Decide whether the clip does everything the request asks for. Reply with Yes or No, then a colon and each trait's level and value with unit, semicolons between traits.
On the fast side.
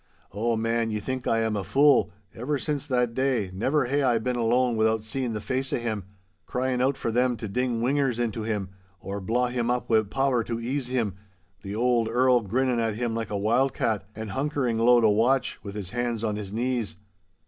Yes: fast, 210 wpm